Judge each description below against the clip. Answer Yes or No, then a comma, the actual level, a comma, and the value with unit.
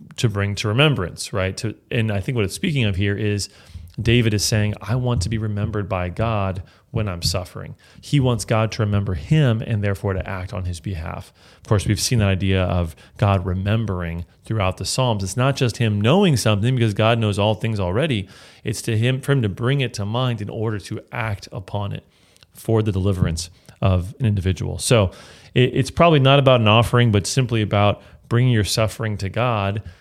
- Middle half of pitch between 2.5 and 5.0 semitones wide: Yes, average, 3.8 semitones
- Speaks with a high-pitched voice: No, low, 110 Hz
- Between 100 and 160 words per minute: No, fast, 205 wpm